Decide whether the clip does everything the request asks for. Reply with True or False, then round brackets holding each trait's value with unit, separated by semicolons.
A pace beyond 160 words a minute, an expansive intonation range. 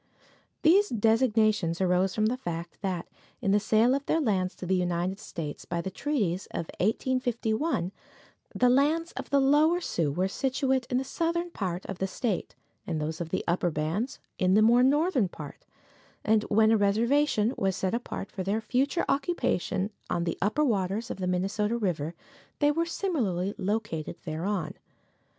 True (170 wpm; 6.2 semitones)